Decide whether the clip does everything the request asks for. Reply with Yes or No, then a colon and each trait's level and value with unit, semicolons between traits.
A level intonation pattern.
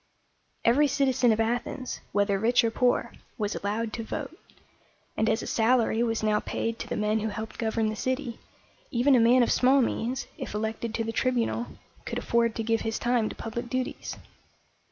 Yes: narrow, 2.1 semitones